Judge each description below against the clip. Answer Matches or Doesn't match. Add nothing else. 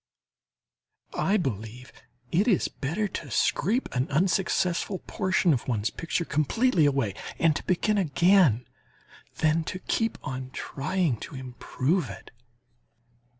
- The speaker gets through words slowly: Matches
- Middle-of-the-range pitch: Matches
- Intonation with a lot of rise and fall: Matches